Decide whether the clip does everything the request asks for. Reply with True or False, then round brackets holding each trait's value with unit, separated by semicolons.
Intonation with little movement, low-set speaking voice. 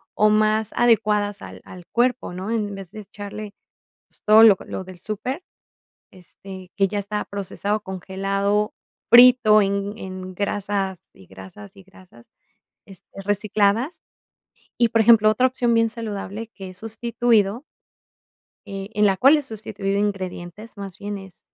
False (2.3 semitones; 205 Hz)